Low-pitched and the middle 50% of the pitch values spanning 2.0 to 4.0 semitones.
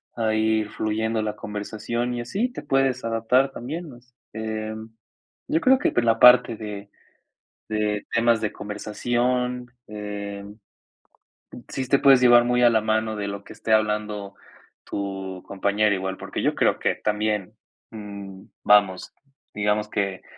Yes: low, 110 Hz; average, 2.7 semitones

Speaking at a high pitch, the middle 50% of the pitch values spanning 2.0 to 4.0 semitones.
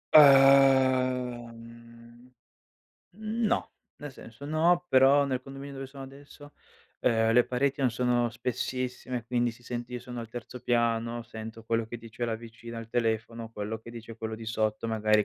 No: low, 120 Hz; average, 2.8 semitones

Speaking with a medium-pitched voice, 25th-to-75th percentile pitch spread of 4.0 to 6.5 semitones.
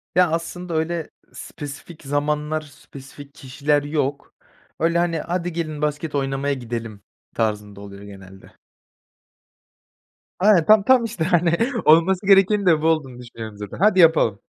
Yes: medium, 150 Hz; average, 4.4 semitones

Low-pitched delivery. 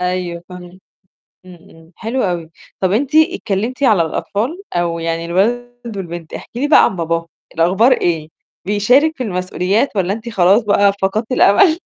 No: high, 195 Hz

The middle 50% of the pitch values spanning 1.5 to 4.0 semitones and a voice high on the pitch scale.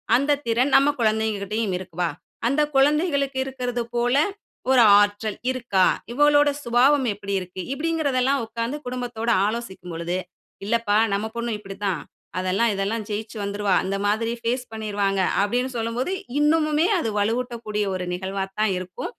No: average, 4.4 semitones; high, 230 Hz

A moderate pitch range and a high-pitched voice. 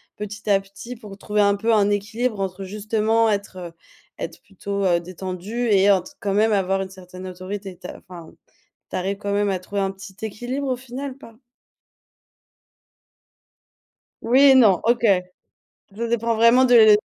Yes: average, 3.0 semitones; high, 205 Hz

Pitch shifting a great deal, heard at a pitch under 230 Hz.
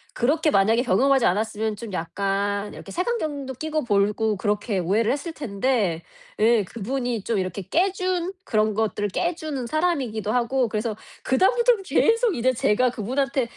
No: wide, 5.8 semitones; high, 235 Hz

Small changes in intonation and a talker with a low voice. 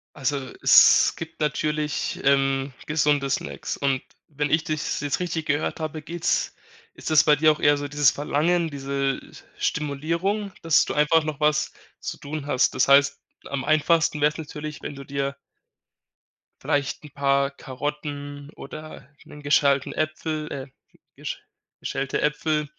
No: narrow, 1.8 semitones; medium, 150 Hz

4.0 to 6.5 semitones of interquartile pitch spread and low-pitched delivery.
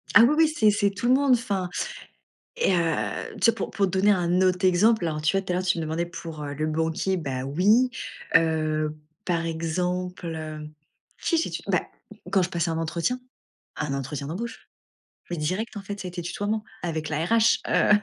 No: average, 4.3 semitones; medium, 180 Hz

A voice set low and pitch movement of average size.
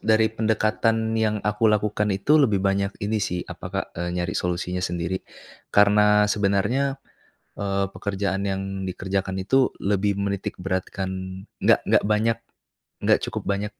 No: low, 100 Hz; narrow, 1.9 semitones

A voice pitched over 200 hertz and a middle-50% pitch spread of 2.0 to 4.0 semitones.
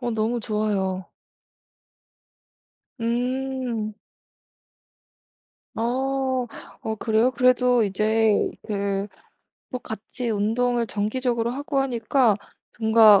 Yes: high, 230 Hz; average, 2.8 semitones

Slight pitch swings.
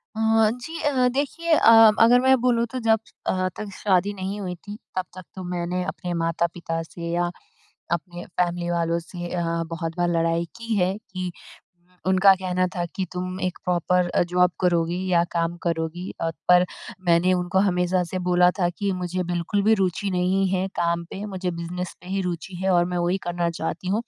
Yes: narrow, 1.8 semitones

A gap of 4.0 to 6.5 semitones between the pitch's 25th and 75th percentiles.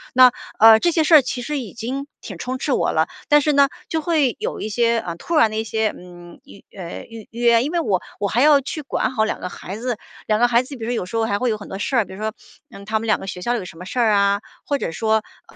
Yes: average, 4.3 semitones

